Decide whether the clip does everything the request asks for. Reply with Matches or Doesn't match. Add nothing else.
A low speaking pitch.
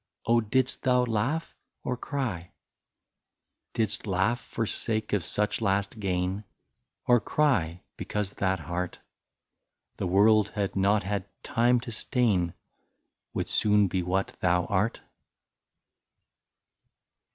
Matches